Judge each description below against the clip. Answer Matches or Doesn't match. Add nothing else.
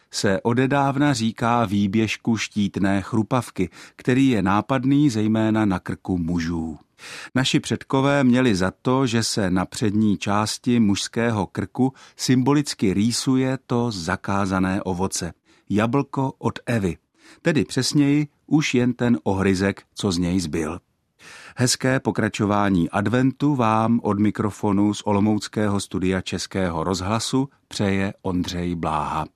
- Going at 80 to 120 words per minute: Matches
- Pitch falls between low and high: Doesn't match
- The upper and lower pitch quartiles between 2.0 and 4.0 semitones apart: Doesn't match